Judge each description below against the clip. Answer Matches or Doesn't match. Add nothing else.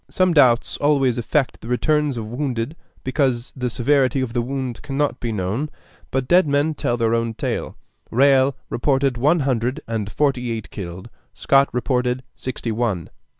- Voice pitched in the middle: Doesn't match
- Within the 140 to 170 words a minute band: Matches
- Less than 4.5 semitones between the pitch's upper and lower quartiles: Matches